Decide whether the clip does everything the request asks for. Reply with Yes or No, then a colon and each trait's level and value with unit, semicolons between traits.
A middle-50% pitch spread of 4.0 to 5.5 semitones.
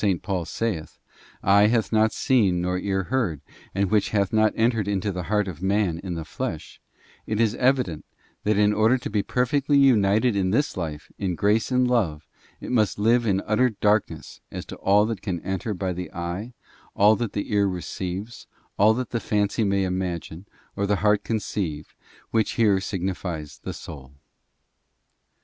No: average, 3.2 semitones